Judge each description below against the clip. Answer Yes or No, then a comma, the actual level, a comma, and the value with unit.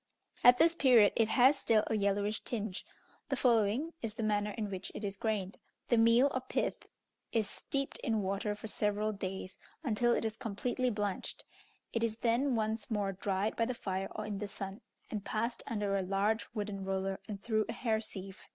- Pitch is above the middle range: Yes, high, 215 Hz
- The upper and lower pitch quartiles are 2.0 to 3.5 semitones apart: Yes, narrow, 2.6 semitones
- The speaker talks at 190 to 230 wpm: Yes, average, 195 wpm